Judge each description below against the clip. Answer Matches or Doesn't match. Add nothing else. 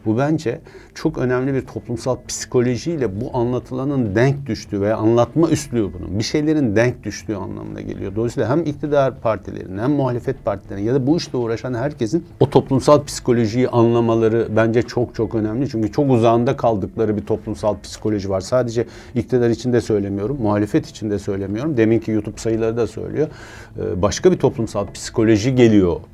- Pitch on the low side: Matches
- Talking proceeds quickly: Matches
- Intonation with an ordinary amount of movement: Matches